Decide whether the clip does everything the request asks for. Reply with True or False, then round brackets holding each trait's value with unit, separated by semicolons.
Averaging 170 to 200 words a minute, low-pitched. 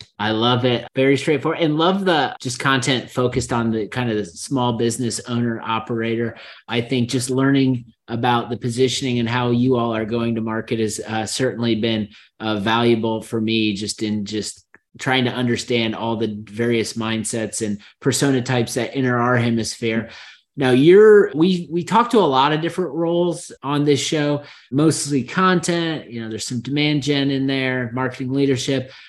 True (175 wpm; 125 Hz)